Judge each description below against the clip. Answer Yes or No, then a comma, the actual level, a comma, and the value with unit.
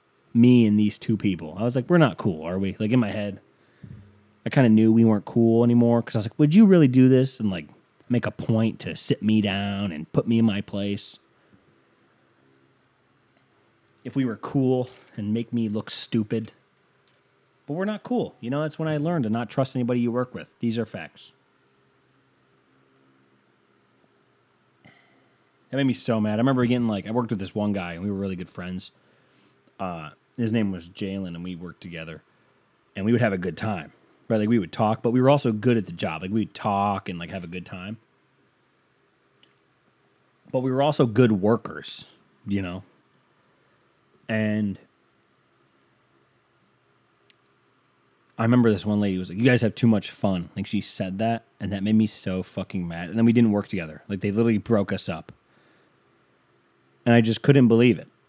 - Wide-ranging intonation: Yes, wide, 7.6 semitones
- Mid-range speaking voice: No, low, 105 Hz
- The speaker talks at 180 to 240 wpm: Yes, average, 195 wpm